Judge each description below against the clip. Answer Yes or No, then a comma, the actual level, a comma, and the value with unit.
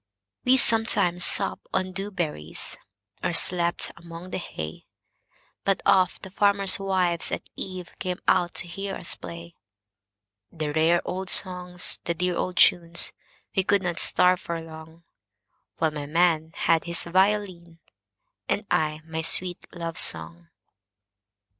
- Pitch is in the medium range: Yes, medium, 170 Hz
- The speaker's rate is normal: No, slow, 120 wpm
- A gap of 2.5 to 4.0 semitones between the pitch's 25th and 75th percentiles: Yes, average, 2.8 semitones